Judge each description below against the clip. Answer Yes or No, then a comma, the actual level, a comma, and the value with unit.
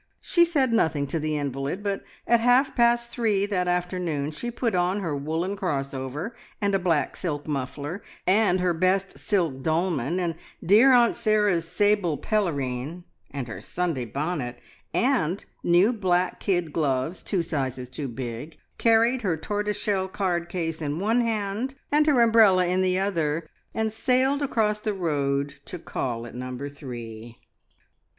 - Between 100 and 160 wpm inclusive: Yes, average, 155 wpm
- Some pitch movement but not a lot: No, wide, 6.4 semitones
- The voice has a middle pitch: Yes, medium, 180 Hz